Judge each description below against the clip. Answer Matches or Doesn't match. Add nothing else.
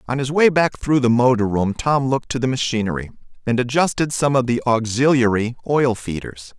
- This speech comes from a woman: Doesn't match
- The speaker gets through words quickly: Doesn't match